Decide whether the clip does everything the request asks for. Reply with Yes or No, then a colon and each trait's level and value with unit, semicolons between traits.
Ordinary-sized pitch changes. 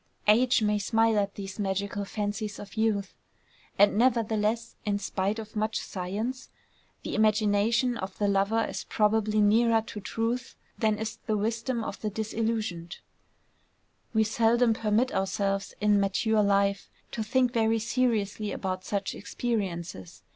No: narrow, 2.0 semitones